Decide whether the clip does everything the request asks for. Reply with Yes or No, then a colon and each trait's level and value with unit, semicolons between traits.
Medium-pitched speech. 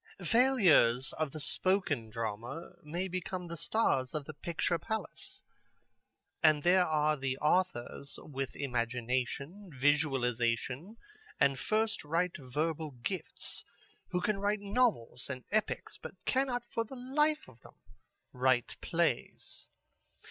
Yes: medium, 155 Hz